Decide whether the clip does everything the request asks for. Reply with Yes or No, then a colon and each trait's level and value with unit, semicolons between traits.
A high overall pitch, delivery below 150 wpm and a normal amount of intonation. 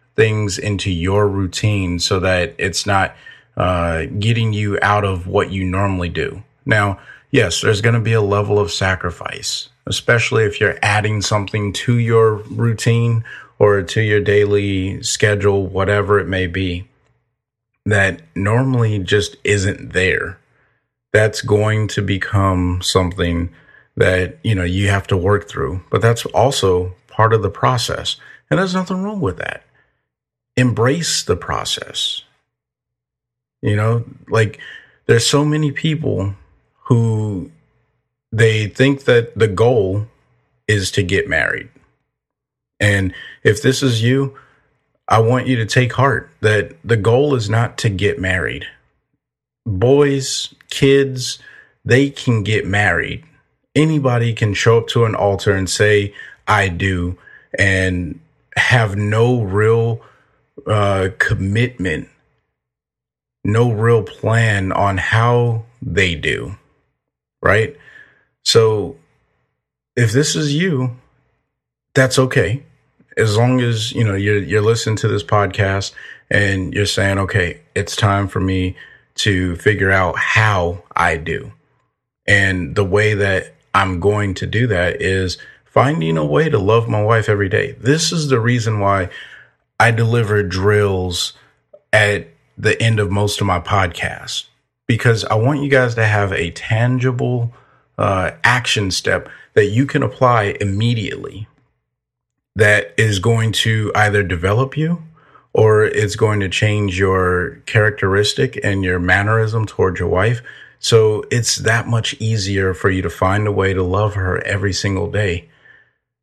No: low, 105 Hz; slow, 135 wpm; average, 3.3 semitones